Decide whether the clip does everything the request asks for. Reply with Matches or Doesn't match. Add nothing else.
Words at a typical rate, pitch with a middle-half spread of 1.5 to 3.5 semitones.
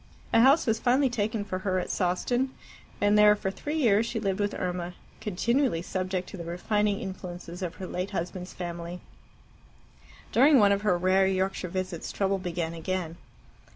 Matches